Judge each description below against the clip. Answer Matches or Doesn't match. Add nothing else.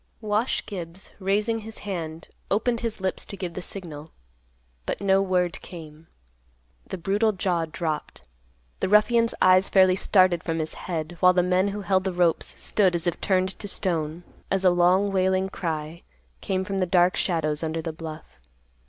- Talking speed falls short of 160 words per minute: Doesn't match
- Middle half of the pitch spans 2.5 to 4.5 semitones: Matches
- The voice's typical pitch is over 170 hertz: Matches